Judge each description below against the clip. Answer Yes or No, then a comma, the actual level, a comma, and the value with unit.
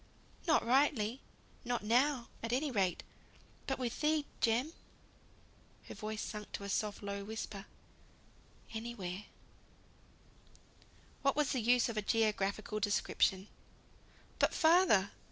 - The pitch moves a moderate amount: Yes, average, 4.0 semitones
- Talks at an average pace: No, slow, 120 wpm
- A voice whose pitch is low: No, high, 225 Hz